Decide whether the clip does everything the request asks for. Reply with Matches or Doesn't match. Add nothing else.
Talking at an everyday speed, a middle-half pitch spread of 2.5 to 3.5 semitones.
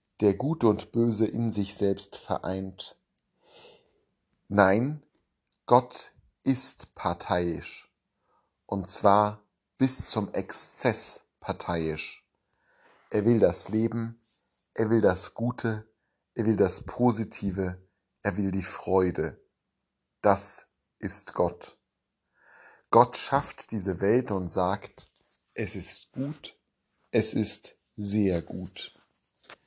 Doesn't match